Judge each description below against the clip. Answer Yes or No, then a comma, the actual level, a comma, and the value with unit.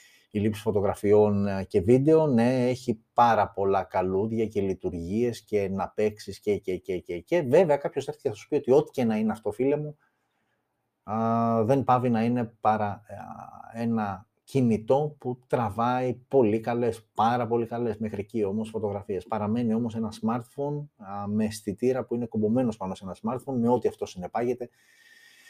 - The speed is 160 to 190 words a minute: Yes, average, 165 wpm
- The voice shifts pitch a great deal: No, average, 2.9 semitones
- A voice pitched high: No, low, 115 Hz